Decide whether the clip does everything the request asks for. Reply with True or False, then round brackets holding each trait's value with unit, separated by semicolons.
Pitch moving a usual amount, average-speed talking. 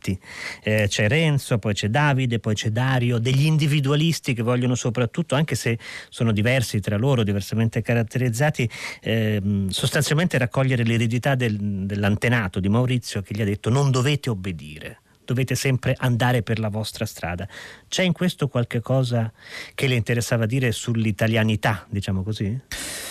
True (3.3 semitones; 145 wpm)